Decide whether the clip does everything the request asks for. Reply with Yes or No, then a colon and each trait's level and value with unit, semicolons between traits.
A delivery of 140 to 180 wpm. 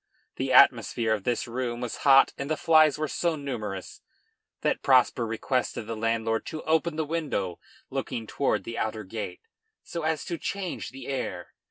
Yes: average, 170 wpm